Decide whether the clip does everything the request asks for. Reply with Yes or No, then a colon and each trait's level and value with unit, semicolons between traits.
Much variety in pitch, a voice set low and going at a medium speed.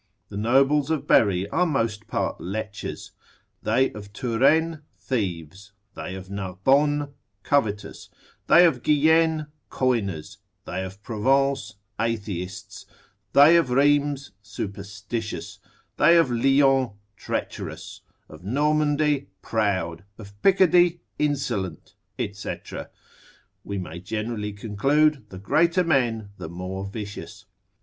No: wide, 6.5 semitones; low, 115 Hz; slow, 105 wpm